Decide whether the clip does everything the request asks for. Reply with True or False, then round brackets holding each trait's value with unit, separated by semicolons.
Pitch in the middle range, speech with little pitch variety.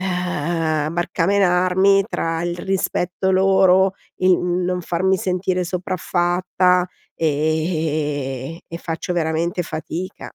True (180 Hz; 2.2 semitones)